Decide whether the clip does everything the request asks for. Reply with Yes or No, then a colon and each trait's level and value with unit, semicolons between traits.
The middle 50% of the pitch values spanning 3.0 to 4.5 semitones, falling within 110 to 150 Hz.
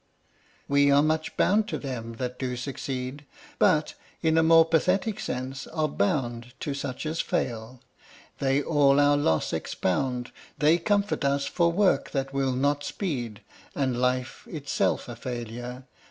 Yes: average, 3.7 semitones; medium, 140 Hz